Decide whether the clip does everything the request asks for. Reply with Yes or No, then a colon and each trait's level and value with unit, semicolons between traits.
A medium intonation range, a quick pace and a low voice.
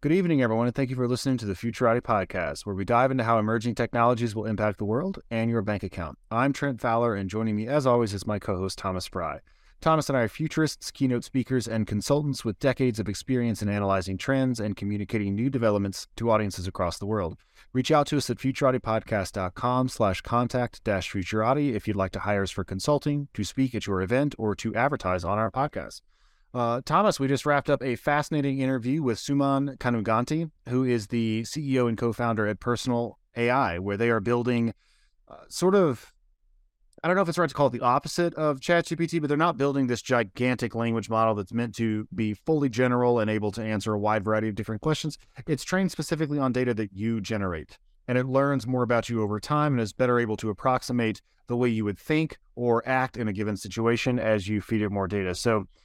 Yes: average, 3.9 semitones; fast, 210 wpm; low, 120 Hz